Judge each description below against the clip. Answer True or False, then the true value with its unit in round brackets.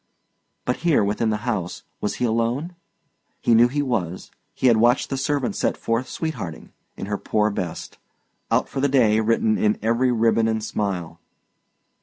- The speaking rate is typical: True (175 wpm)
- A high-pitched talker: False (115 Hz)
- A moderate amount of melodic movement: True (3.1 semitones)